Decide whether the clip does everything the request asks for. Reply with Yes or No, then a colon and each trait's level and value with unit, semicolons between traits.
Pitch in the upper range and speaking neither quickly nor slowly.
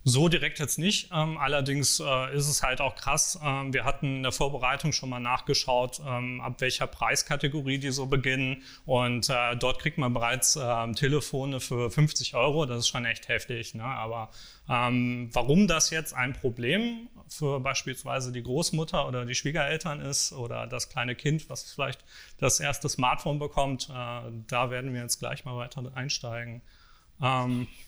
No: low, 130 Hz; average, 155 wpm